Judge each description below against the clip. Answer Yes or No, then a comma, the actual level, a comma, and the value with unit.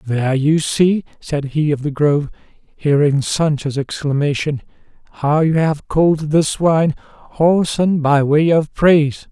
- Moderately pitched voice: Yes, medium, 150 Hz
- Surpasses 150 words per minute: No, average, 140 wpm